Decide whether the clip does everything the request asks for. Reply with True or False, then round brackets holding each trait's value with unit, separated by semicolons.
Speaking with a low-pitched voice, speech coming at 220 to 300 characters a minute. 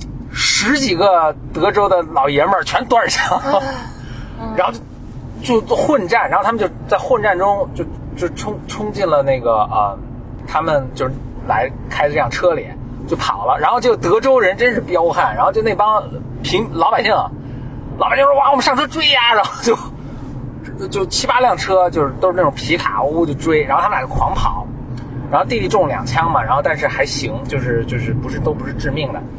False (155 Hz; 275 characters per minute)